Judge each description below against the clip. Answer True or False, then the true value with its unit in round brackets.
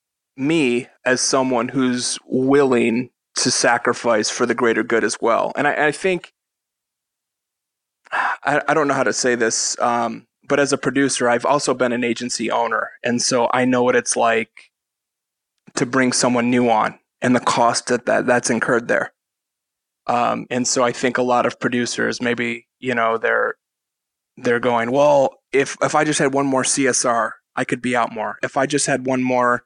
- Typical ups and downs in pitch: False (2.3 semitones)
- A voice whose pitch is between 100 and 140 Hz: True (125 Hz)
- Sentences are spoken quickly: False (180 wpm)